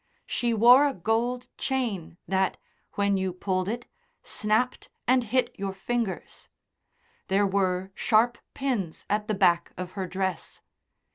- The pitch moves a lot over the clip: No, average, 4.1 semitones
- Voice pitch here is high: Yes, high, 205 Hz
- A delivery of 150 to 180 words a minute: No, slow, 135 wpm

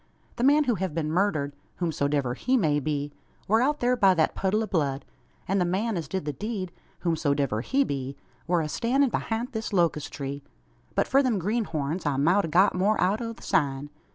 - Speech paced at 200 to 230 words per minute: Yes, fast, 205 wpm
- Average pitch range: No, wide, 7.1 semitones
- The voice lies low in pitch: No, medium, 180 Hz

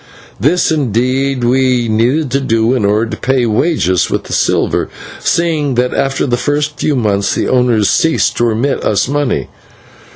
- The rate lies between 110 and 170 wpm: Yes, average, 165 wpm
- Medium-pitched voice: No, low, 125 Hz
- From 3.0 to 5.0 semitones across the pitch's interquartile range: Yes, average, 3.9 semitones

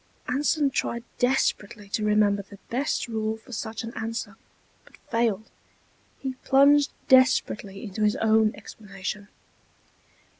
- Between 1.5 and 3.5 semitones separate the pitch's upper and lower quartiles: Yes, average, 3.2 semitones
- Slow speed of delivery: Yes, slow, 120 wpm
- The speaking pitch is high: Yes, high, 220 Hz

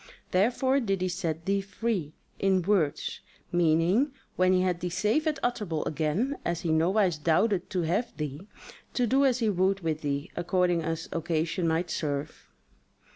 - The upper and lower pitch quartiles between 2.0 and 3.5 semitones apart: No, average, 4.0 semitones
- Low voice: No, medium, 180 Hz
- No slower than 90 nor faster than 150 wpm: No, average, 165 wpm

